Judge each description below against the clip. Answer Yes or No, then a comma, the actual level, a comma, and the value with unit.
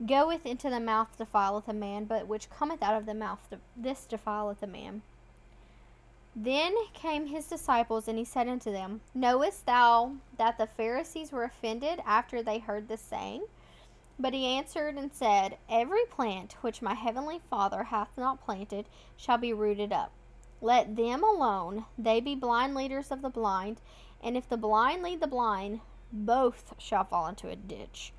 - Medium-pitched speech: No, high, 235 Hz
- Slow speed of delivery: No, average, 170 wpm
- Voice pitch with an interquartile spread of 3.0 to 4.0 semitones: Yes, average, 3.7 semitones